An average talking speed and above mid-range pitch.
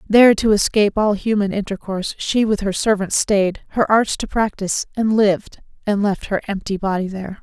Yes: average, 185 wpm; high, 205 Hz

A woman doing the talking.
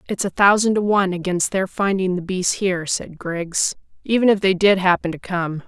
Yes: female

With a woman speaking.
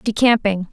Yes: female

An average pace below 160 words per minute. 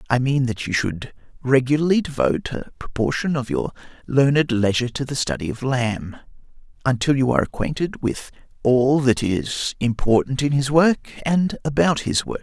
No: average, 165 wpm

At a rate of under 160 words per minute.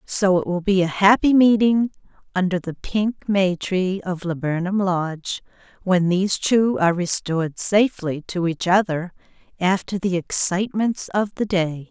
Yes: average, 150 wpm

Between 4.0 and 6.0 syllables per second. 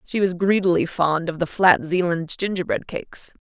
Yes: 5.0 syllables/s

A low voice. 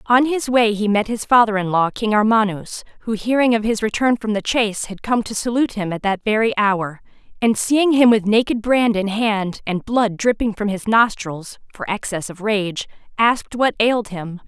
No: high, 215 Hz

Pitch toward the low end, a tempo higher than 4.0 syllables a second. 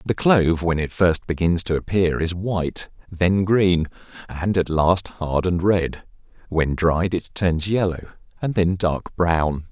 No: very low, 90 Hz; 3.9 syllables/s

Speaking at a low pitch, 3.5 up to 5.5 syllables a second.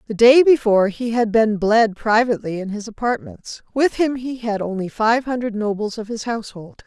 No: high, 220 Hz; 5.2 syllables/s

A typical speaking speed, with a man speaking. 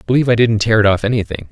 No: fast, 315 wpm; male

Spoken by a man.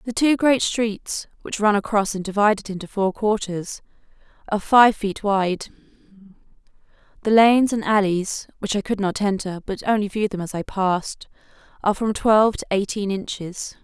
No: female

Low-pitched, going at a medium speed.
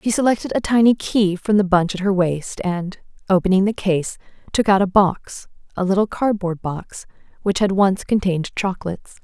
No: high, 195 Hz; average, 180 wpm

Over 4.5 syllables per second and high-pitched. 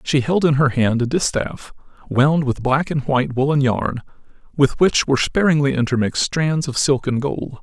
No: 5.0 syllables/s; medium, 140 Hz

